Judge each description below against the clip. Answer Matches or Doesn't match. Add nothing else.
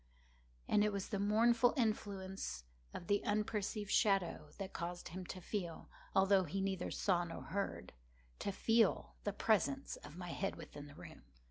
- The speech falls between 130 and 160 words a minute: Matches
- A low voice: Doesn't match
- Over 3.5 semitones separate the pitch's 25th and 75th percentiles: Doesn't match